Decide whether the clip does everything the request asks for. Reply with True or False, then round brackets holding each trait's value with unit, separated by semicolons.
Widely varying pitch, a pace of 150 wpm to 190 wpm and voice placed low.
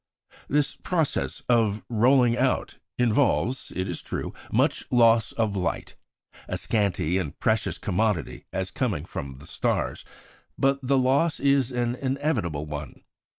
False (5.8 semitones; 135 wpm; 115 Hz)